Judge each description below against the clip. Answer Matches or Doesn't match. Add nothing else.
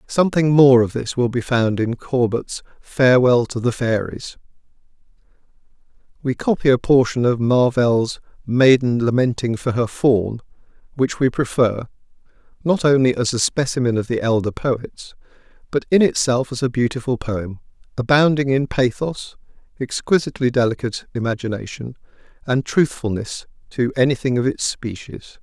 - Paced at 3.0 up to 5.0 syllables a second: Matches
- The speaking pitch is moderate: Doesn't match